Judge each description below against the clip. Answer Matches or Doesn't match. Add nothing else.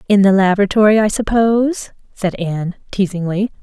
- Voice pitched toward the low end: Doesn't match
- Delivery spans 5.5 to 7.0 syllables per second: Matches